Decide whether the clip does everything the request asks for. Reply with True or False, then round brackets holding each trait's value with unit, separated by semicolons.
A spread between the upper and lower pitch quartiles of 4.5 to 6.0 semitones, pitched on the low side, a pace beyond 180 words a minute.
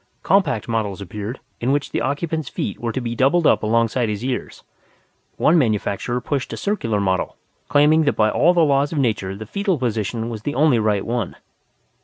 True (5.2 semitones; 120 Hz; 190 wpm)